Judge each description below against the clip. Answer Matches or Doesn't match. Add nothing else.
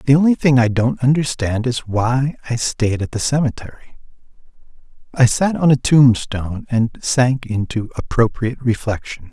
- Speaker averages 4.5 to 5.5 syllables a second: Matches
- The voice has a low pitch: Matches